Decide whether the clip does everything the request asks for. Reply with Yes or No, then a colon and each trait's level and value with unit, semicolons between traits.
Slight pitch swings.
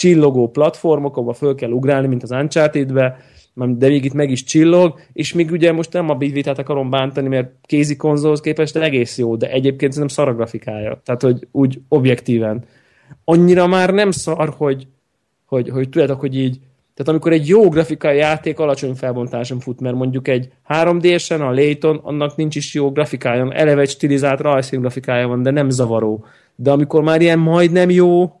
No: average, 3.4 semitones